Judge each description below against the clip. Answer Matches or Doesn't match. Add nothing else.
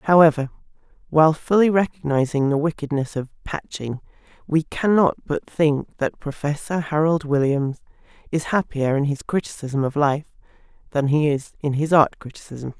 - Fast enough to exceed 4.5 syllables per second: Matches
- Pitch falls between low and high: Matches